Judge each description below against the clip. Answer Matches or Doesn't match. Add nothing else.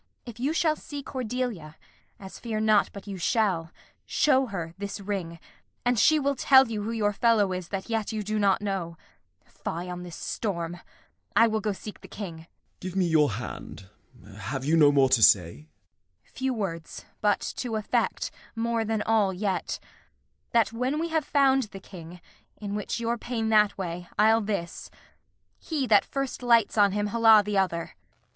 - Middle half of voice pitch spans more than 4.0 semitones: Matches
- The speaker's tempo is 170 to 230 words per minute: Matches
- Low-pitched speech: Doesn't match